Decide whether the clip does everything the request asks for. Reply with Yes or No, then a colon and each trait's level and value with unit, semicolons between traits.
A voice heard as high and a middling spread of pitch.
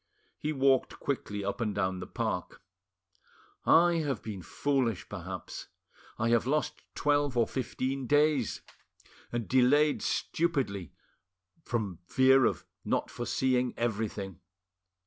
No: low, 125 Hz; average, 4.8 semitones